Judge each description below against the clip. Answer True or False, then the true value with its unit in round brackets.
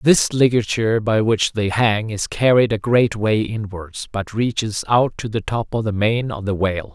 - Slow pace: False (205 wpm)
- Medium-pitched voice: False (110 Hz)